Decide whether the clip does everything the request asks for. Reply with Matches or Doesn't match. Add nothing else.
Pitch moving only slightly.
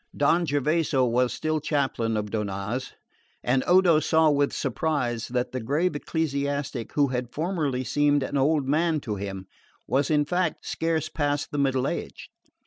Doesn't match